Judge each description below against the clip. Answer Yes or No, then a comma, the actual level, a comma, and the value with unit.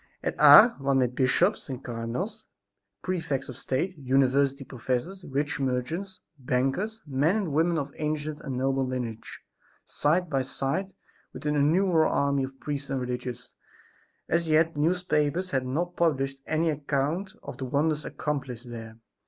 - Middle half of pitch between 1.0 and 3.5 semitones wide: No, average, 3.9 semitones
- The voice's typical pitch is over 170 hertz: No, medium, 140 Hz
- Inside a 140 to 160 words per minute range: Yes, average, 150 wpm